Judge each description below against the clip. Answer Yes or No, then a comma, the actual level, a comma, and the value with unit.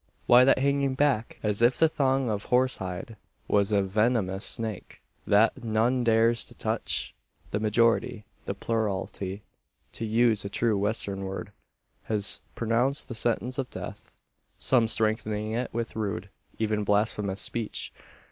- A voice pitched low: Yes, low, 110 Hz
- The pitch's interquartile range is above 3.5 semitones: No, average, 2.7 semitones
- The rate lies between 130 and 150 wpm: Yes, average, 145 wpm